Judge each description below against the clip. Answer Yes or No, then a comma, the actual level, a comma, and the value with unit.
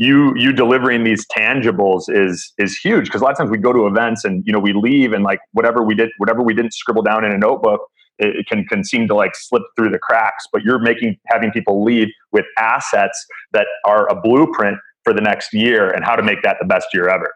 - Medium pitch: No, low, 115 Hz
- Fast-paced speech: Yes, fast, 245 wpm